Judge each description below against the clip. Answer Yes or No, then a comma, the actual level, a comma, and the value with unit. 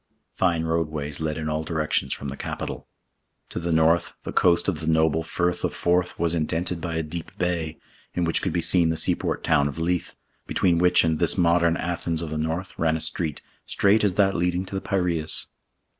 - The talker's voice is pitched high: No, very low, 85 Hz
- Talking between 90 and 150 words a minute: No, fast, 205 wpm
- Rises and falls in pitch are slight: Yes, narrow, 1.7 semitones